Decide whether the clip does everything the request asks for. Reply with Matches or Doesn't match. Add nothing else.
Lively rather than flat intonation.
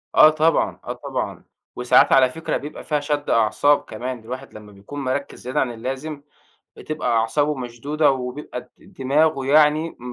Doesn't match